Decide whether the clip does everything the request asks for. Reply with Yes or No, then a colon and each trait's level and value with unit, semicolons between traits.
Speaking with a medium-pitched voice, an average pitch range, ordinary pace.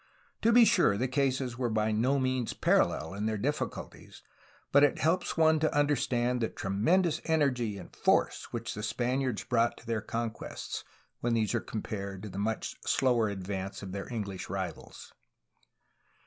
No: low, 120 Hz; average, 4.4 semitones; average, 160 wpm